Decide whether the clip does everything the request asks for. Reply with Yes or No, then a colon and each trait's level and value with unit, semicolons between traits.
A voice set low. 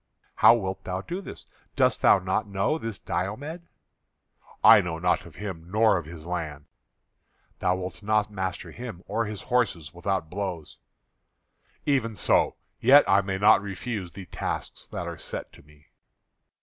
Yes: very low, 95 Hz